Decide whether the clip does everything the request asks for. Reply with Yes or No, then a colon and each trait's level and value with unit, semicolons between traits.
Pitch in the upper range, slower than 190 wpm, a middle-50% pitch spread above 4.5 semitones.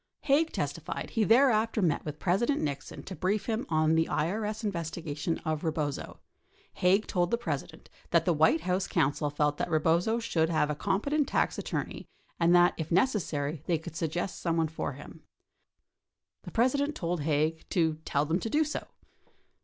No: medium, 170 Hz; average, 170 wpm; average, 5.3 semitones